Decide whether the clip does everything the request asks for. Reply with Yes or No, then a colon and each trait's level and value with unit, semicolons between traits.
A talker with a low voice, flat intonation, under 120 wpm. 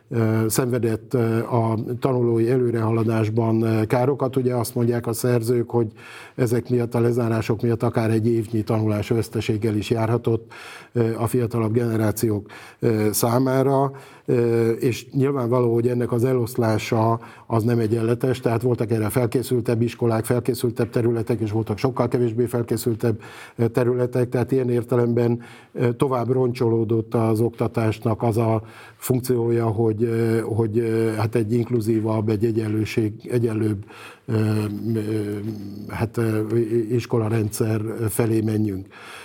Yes: low, 115 Hz; narrow, 1.5 semitones; average, 110 wpm